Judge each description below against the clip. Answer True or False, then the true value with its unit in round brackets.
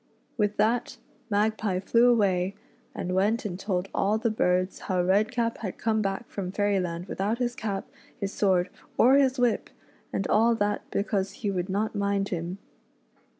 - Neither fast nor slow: True (150 wpm)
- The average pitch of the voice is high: True (200 Hz)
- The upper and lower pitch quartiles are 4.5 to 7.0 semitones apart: False (2.7 semitones)